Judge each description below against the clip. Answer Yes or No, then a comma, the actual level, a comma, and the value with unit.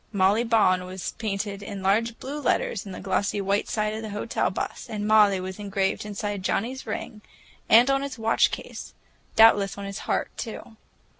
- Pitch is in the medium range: No, high, 210 Hz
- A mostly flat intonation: Yes, narrow, 2.2 semitones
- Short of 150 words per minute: No, average, 175 wpm